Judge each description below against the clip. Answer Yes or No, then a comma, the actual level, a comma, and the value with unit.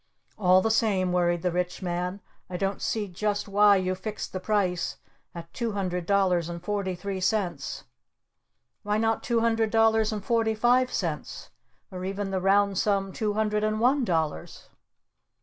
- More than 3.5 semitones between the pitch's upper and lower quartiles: No, average, 3.1 semitones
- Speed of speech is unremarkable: Yes, average, 165 wpm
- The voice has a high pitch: Yes, high, 200 Hz